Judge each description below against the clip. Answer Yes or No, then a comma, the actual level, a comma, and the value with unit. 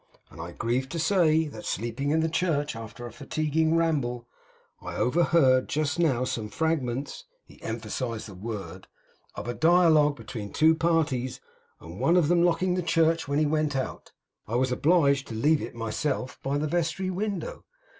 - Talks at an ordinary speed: Yes, average, 170 wpm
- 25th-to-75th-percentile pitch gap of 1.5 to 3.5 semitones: No, average, 5.2 semitones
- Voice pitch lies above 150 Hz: No, medium, 145 Hz